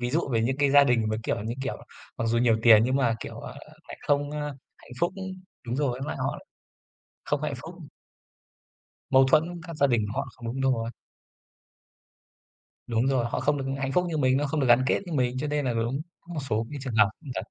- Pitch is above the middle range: No, low, 130 Hz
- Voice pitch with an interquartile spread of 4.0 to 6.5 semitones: No, average, 3.6 semitones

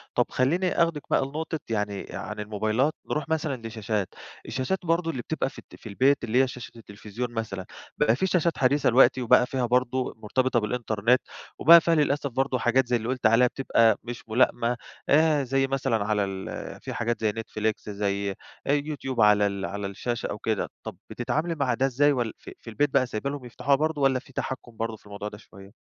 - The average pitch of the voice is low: Yes, low, 125 Hz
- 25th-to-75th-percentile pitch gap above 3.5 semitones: Yes, average, 4.1 semitones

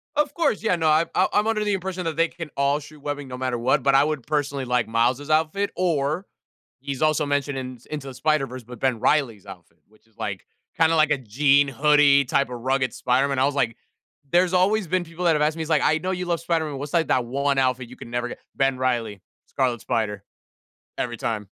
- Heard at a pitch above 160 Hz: No, medium, 140 Hz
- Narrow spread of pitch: No, average, 4.1 semitones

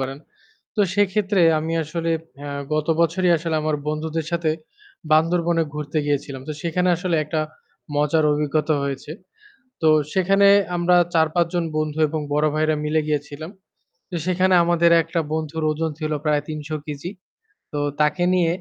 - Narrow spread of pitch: Yes, narrow, 2.2 semitones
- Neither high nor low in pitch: Yes, medium, 160 Hz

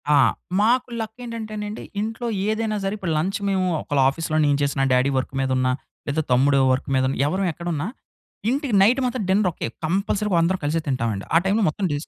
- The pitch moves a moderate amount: No, wide, 6.9 semitones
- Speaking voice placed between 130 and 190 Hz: Yes, medium, 185 Hz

